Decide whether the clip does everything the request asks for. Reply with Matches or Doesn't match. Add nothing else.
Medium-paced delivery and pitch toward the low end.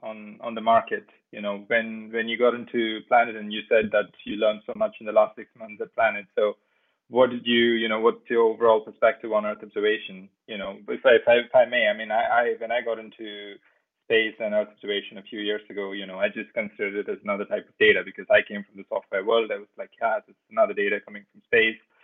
Doesn't match